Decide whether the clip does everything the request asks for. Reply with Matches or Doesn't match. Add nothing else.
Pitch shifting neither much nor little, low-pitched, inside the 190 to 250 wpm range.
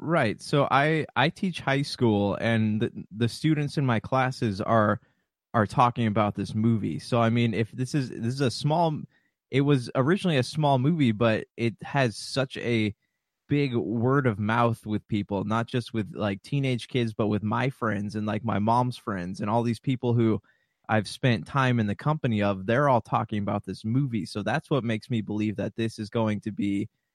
Matches